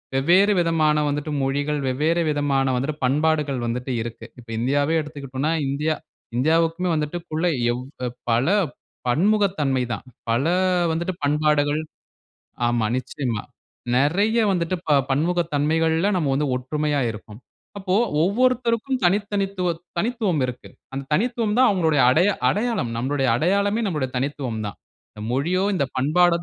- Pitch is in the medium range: Yes, medium, 150 Hz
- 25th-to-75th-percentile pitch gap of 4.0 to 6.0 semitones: Yes, average, 4.9 semitones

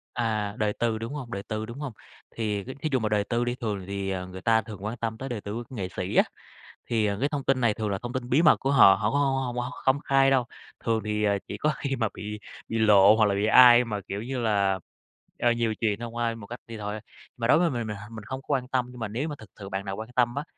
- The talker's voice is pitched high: No, low, 115 Hz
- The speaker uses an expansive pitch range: No, average, 3.1 semitones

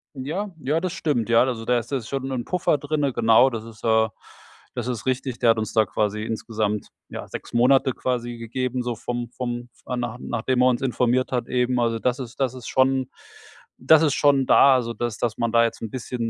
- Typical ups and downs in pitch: No, narrow, 2.2 semitones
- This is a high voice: No, low, 125 Hz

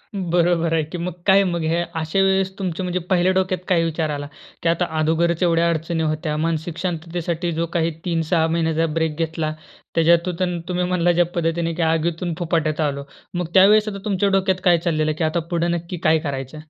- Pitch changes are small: Yes, narrow, 1.7 semitones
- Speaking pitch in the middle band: Yes, medium, 170 Hz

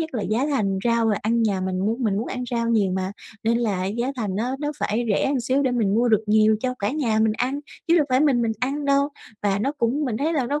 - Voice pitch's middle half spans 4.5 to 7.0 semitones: No, average, 3.9 semitones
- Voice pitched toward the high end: Yes, high, 235 Hz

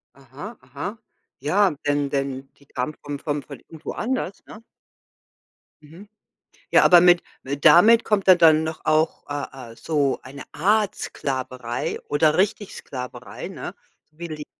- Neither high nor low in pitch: Yes, medium, 155 Hz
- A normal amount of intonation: Yes, average, 5.0 semitones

